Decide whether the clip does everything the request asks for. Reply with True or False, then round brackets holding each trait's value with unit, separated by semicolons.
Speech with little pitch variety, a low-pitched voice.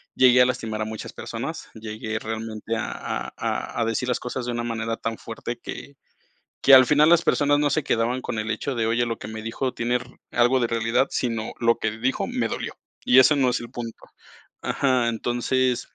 True (2.2 semitones; 120 Hz)